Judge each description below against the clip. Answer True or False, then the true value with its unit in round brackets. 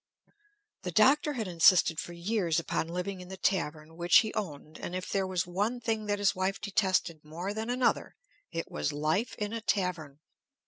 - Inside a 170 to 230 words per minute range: True (185 wpm)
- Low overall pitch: False (185 Hz)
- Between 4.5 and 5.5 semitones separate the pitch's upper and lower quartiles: False (4.0 semitones)